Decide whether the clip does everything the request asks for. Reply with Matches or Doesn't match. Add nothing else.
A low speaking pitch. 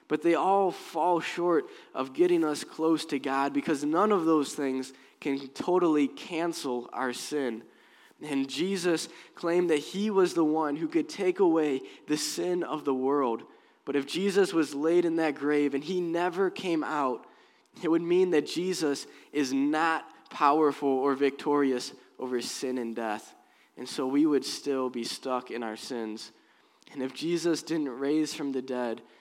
Doesn't match